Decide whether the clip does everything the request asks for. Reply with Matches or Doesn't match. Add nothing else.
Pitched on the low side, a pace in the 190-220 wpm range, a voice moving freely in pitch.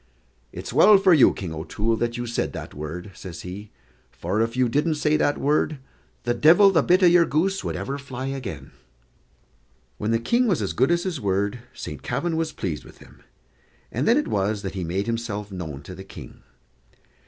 Matches